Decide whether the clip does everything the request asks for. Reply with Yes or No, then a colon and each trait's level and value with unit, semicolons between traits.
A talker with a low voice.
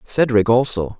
Yes: low, 115 Hz